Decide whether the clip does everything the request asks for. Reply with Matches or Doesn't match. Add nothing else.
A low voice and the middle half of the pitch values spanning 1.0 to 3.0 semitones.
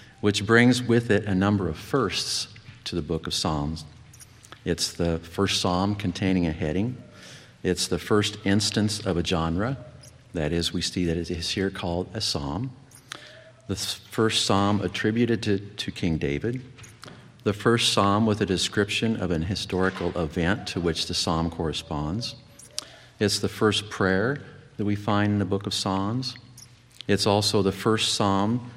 Doesn't match